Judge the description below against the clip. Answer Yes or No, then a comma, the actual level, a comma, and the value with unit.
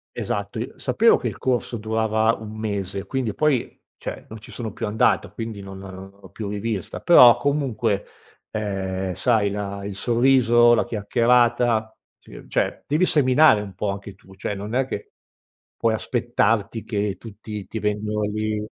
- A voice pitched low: Yes, low, 110 Hz